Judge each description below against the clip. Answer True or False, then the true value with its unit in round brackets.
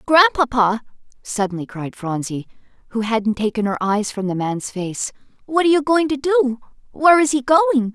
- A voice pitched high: True (245 Hz)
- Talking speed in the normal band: True (165 wpm)